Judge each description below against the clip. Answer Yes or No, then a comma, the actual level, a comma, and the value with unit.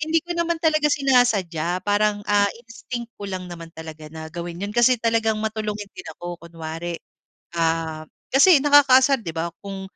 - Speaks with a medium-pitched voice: No, high, 205 Hz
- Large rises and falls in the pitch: Yes, wide, 6.9 semitones